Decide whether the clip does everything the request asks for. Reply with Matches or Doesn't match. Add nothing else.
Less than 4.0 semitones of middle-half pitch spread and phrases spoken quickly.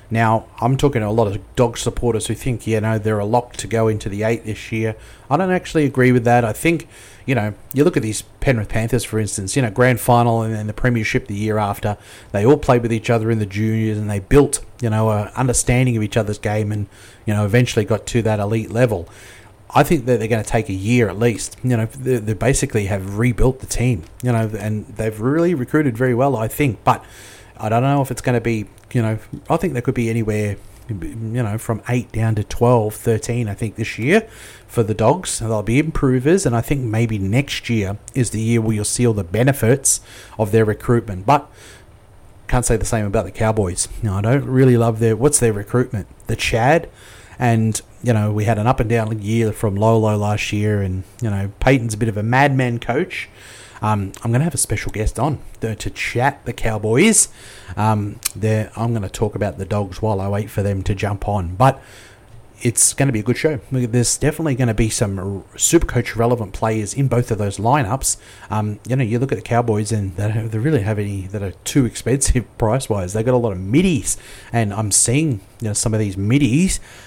Matches